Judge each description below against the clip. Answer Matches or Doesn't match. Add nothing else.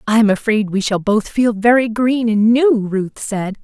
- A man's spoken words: Doesn't match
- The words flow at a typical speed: Doesn't match